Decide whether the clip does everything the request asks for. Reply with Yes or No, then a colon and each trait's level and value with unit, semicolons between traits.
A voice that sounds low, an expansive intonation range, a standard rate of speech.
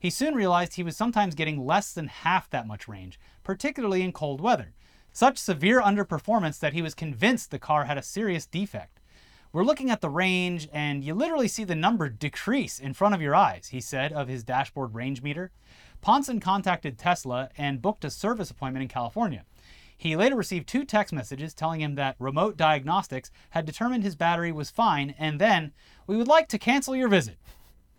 No: medium, 170 Hz; wide, 6.7 semitones; average, 195 wpm